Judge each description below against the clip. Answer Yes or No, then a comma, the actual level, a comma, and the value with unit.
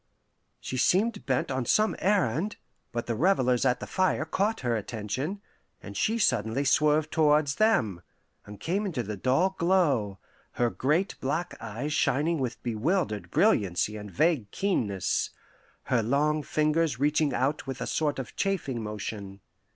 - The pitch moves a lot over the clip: Yes, wide, 6.6 semitones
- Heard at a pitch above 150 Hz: No, medium, 140 Hz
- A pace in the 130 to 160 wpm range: Yes, average, 150 wpm